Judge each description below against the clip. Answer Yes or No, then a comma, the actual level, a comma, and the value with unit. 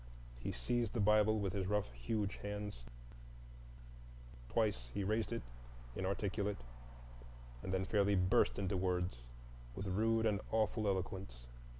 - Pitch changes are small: Yes, narrow, 2.3 semitones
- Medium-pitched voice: No, low, 100 Hz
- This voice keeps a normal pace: No, slow, 125 wpm